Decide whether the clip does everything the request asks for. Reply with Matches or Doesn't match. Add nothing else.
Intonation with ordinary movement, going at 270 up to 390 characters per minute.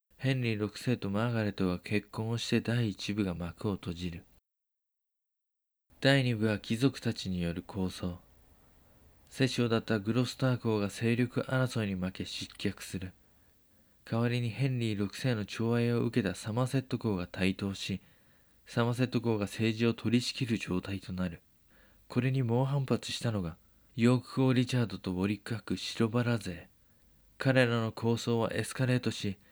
Matches